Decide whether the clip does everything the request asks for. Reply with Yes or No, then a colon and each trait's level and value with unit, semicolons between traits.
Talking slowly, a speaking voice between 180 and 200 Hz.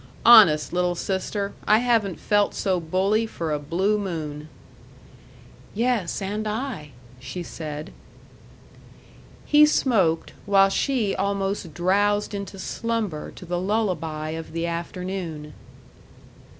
Yes: slow, 115 wpm; high, 190 Hz